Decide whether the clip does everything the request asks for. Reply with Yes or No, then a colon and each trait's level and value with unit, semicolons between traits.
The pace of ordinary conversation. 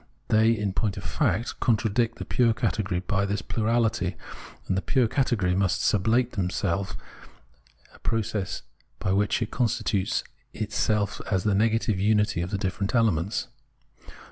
Yes: average, 150 wpm